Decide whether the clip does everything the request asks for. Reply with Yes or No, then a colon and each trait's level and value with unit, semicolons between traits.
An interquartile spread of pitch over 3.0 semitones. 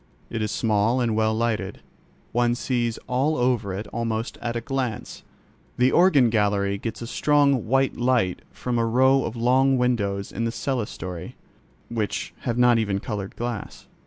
No: average, 2.7 semitones